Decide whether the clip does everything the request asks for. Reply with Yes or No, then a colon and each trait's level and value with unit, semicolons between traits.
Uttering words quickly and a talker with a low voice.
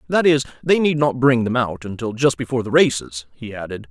Yes: fast, 230 wpm; low, 125 Hz